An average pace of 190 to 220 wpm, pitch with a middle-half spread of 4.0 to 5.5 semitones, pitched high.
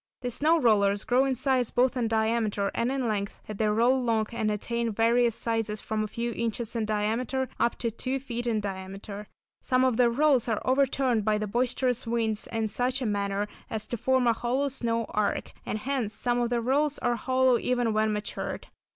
No: fast, 205 wpm; average, 2.9 semitones; high, 235 Hz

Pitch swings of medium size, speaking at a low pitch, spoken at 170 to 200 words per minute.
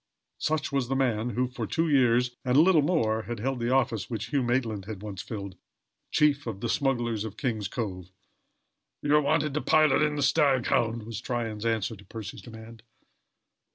Yes: average, 4.1 semitones; low, 120 Hz; average, 190 wpm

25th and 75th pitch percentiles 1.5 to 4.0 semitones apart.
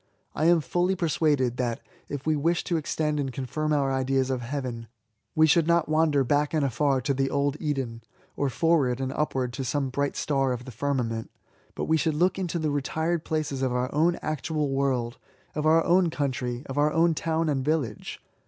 Yes: average, 3.2 semitones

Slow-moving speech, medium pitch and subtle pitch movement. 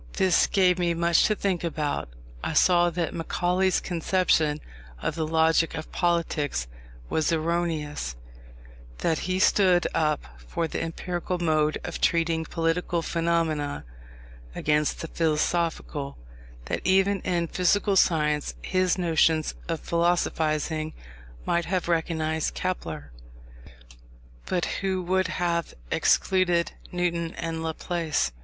Yes: slow, 115 wpm; medium, 170 Hz; narrow, 2.1 semitones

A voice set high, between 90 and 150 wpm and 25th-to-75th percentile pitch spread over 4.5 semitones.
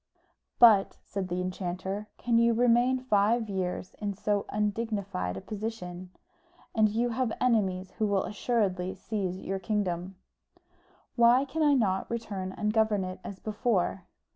No: high, 210 Hz; average, 145 wpm; average, 3.6 semitones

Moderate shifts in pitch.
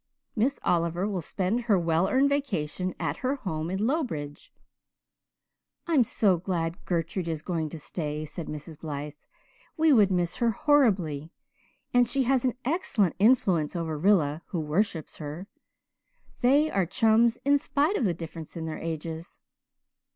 No: wide, 6.8 semitones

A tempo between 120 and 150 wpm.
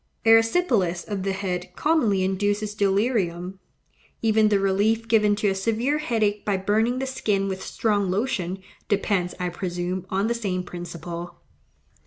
Yes: average, 145 wpm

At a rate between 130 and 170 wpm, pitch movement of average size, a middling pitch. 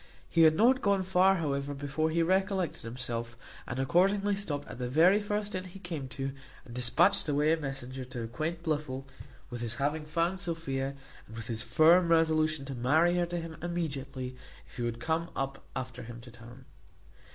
No: average, 185 wpm; average, 5.0 semitones; medium, 155 Hz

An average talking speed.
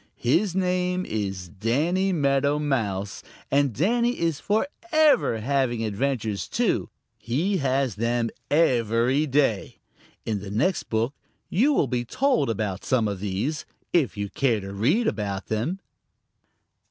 No: slow, 130 wpm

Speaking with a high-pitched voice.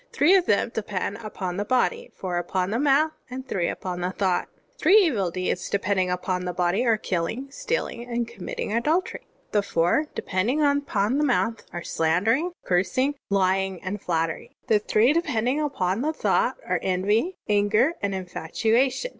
Yes: high, 210 Hz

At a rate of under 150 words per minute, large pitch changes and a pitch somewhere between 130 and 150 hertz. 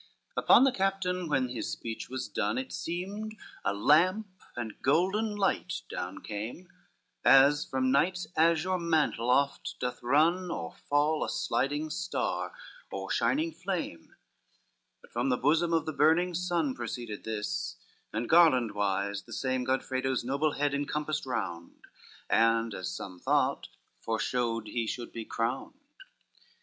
Yes: average, 140 wpm; wide, 6.9 semitones; medium, 140 Hz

